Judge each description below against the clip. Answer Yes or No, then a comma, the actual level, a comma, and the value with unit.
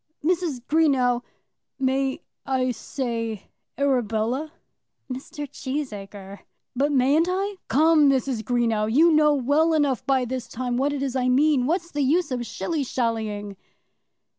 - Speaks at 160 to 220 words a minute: No, slow, 135 wpm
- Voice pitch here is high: Yes, very high, 265 Hz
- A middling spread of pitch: Yes, average, 3.6 semitones